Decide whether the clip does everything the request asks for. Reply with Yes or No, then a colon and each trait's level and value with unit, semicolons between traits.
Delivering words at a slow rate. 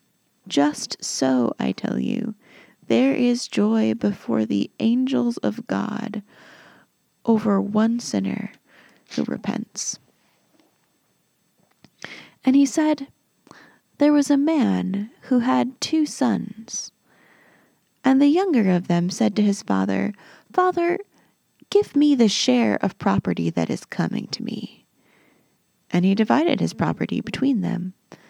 Yes: slow, 120 wpm